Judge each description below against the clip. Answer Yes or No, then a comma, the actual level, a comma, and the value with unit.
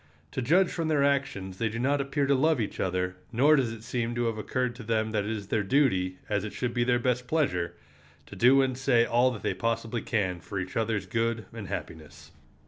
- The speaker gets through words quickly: Yes, fast, 230 wpm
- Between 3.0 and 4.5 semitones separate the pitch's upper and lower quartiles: Yes, average, 4.0 semitones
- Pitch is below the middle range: Yes, low, 115 Hz